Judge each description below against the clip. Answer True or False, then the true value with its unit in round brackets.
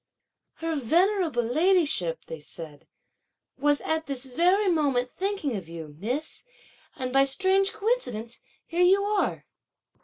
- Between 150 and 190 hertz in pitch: False (295 Hz)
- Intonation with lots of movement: True (7.6 semitones)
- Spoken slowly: True (130 wpm)